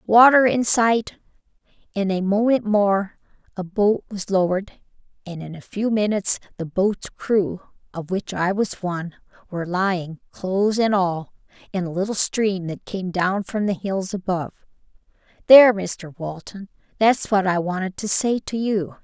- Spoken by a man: No, female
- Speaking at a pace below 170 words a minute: Yes, average, 160 wpm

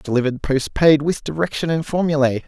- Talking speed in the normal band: Yes, average, 145 wpm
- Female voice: No, male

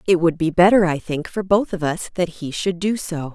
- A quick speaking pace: Yes, fast, 270 wpm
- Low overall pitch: No, medium, 175 Hz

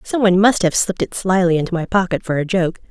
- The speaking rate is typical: No, fast, 270 wpm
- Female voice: Yes, female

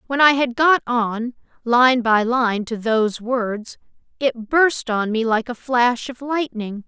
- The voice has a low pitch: No, high, 240 Hz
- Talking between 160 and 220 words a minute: Yes, average, 175 wpm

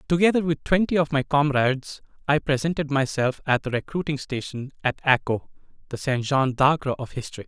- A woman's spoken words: No, male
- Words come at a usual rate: Yes, average, 170 wpm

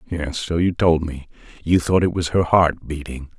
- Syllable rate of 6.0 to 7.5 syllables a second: No, 4.7 syllables/s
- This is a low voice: Yes, very low, 80 Hz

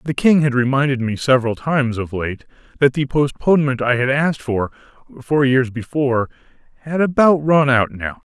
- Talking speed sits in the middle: Yes, average, 175 wpm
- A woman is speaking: No, male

